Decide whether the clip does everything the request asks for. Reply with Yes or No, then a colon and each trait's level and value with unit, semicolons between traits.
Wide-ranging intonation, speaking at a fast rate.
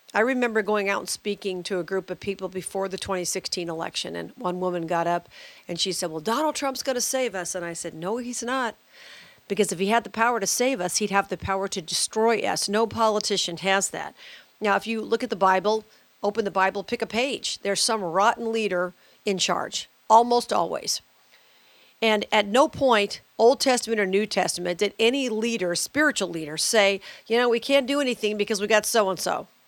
No: average, 3.5 semitones; fast, 210 wpm